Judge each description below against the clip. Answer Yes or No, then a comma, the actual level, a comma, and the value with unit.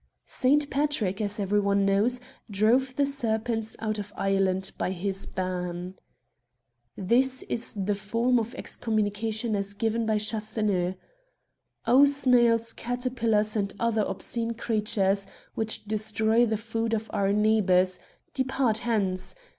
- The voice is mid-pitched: No, high, 220 Hz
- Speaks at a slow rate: Yes, slow, 130 wpm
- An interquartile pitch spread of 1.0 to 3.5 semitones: Yes, average, 2.8 semitones